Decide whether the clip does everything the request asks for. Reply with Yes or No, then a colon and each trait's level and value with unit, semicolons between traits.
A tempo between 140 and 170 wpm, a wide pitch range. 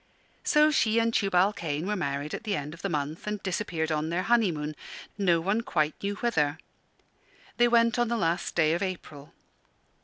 No: average, 185 wpm; wide, 5.7 semitones